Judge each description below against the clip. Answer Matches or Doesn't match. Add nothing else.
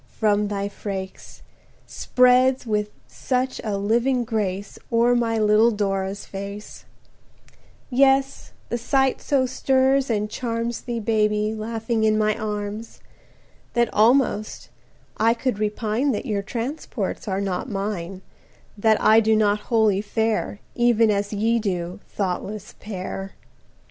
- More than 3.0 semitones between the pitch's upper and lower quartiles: Doesn't match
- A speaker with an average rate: Doesn't match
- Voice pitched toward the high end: Matches